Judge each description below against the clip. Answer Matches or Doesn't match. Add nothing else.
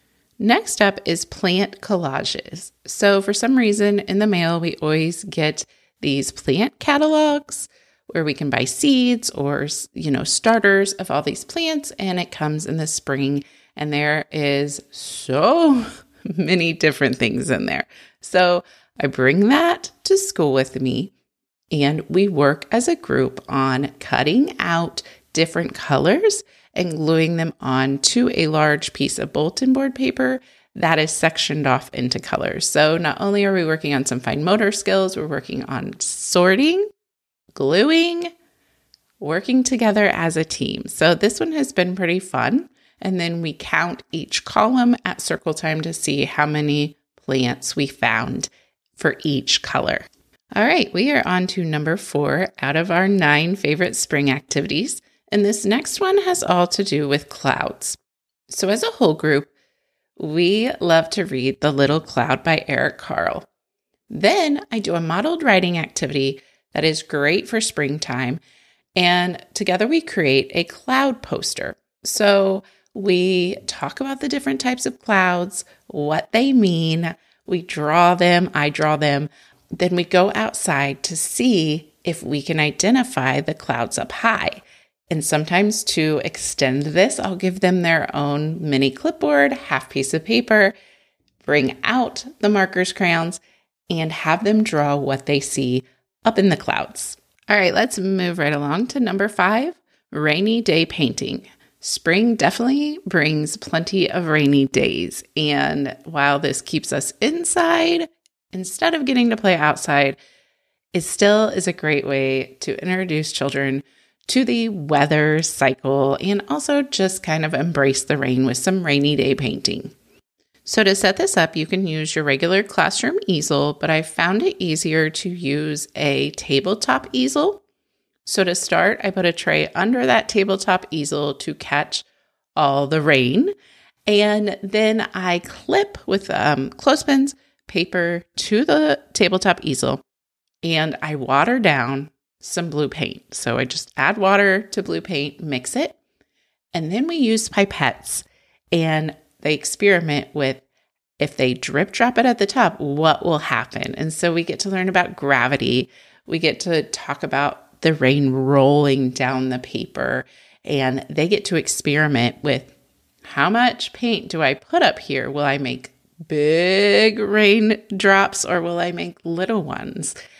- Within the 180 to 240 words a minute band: Doesn't match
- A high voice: Doesn't match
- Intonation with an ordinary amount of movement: Doesn't match